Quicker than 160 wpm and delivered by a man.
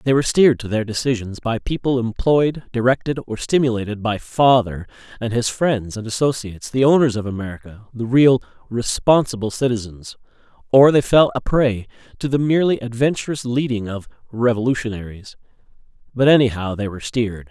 No: average, 150 wpm; male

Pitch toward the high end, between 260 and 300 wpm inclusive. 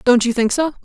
Yes: very high, 255 Hz; fast, 285 wpm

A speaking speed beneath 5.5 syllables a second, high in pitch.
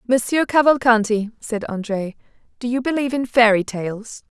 Yes: 5.2 syllables/s; high, 235 Hz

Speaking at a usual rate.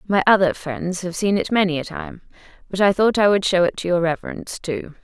No: fast, 240 wpm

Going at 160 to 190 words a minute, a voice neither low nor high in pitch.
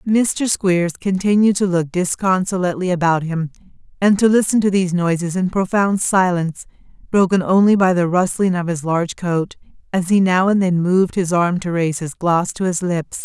Yes: average, 185 wpm; medium, 180 Hz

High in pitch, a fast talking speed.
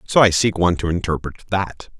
No: very low, 95 Hz; fast, 210 wpm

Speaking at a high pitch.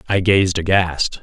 No: very low, 90 Hz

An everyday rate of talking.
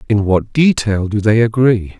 Yes: average, 180 wpm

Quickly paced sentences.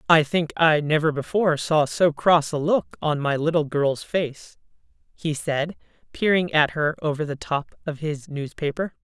No: average, 175 wpm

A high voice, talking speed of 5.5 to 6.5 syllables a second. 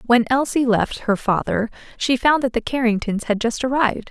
No: high, 240 Hz; 5.2 syllables/s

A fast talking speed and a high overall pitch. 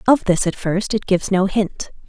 Yes: fast, 230 wpm; high, 195 Hz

